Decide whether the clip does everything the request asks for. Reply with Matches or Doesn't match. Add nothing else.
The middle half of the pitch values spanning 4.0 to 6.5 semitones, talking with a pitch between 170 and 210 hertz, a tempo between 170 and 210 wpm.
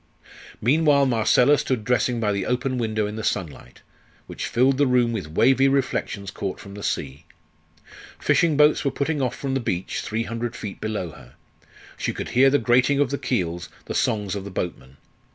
Doesn't match